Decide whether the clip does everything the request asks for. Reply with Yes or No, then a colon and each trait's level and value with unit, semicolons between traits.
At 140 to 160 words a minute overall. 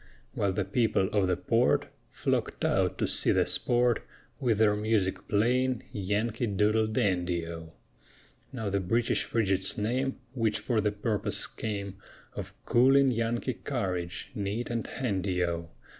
Yes: average, 145 wpm